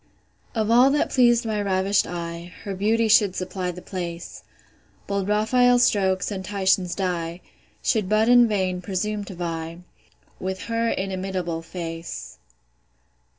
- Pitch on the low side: No, high, 190 Hz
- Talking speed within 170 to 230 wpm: No, slow, 135 wpm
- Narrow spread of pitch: No, average, 3.2 semitones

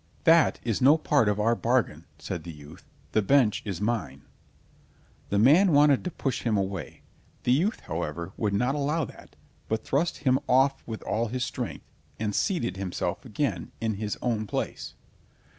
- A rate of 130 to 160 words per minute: No, average, 170 wpm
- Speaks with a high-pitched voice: No, low, 115 Hz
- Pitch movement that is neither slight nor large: No, wide, 5.9 semitones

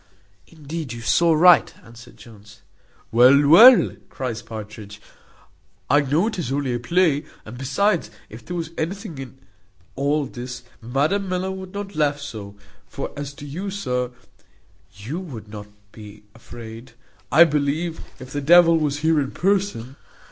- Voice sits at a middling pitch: Yes, medium, 145 Hz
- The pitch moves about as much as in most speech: No, wide, 5.9 semitones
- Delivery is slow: No, average, 150 wpm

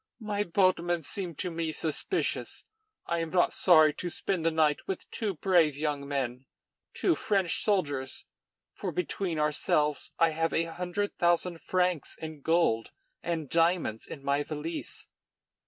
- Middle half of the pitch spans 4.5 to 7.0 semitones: No, average, 3.2 semitones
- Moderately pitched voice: Yes, medium, 165 Hz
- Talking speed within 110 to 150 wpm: Yes, average, 145 wpm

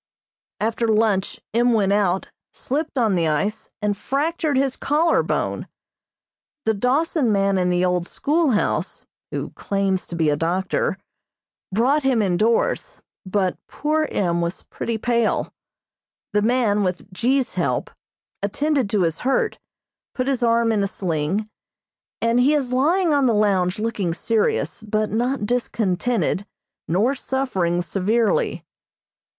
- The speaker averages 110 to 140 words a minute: Yes, slow, 135 wpm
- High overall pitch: Yes, high, 220 Hz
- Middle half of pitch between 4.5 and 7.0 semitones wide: Yes, average, 5.2 semitones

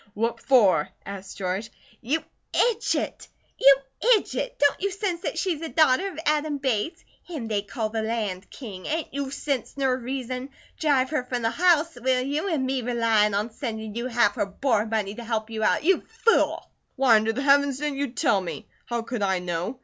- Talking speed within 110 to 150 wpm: No, average, 195 wpm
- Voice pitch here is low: No, very high, 250 Hz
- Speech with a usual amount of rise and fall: Yes, average, 4.7 semitones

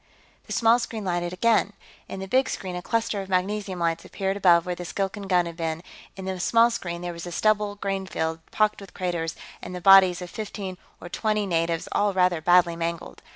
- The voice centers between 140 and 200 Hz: Yes, medium, 185 Hz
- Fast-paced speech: Yes, fast, 210 wpm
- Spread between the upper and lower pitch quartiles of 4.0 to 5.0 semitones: No, average, 2.8 semitones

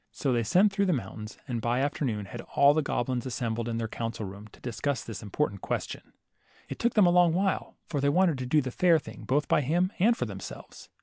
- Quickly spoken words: Yes, fast, 250 wpm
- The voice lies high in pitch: No, low, 135 Hz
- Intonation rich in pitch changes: Yes, wide, 6.6 semitones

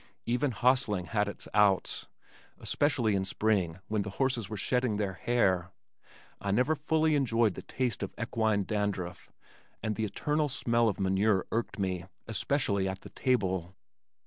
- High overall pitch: No, low, 110 Hz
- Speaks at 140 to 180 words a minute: Yes, average, 150 wpm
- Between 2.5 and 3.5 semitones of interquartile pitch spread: No, average, 4.3 semitones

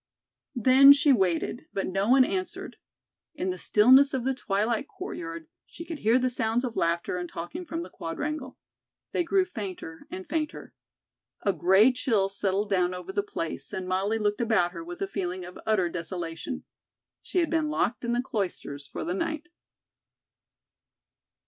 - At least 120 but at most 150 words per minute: No, average, 170 wpm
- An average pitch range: No, wide, 6.6 semitones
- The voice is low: No, high, 210 Hz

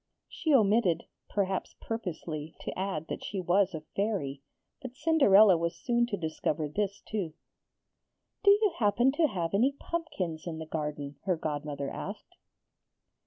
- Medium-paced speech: Yes, average, 145 wpm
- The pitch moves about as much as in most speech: No, wide, 6.5 semitones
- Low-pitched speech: No, high, 190 Hz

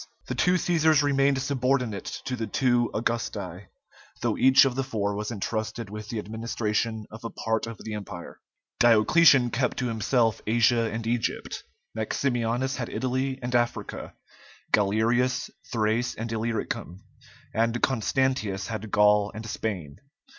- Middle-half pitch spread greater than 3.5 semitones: No, average, 2.9 semitones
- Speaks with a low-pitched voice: Yes, low, 115 Hz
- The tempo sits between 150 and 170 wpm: No, average, 140 wpm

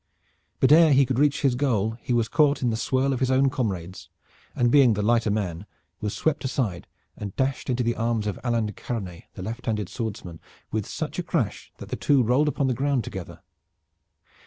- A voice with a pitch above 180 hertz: No, low, 120 Hz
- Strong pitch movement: No, average, 4.1 semitones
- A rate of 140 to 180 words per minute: No, fast, 205 wpm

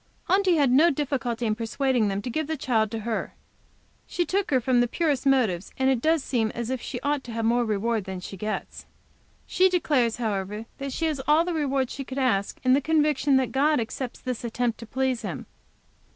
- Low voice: No, very high, 255 Hz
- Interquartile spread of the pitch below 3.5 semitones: No, average, 4.1 semitones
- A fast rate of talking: Yes, fast, 210 wpm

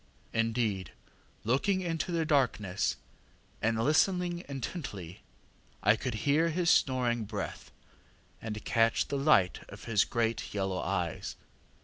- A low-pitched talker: Yes, low, 120 Hz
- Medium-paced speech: No, slow, 120 wpm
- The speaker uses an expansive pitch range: Yes, wide, 6.4 semitones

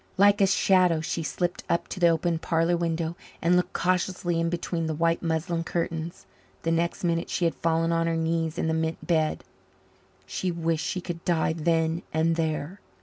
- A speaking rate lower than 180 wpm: No, average, 190 wpm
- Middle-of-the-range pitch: Yes, medium, 165 Hz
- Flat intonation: Yes, narrow, 1.2 semitones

